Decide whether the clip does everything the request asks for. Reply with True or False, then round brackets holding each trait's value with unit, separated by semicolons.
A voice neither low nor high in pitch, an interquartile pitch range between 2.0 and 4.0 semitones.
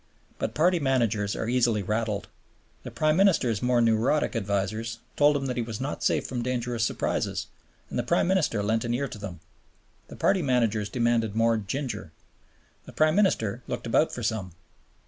False (115 Hz; 3.6 semitones)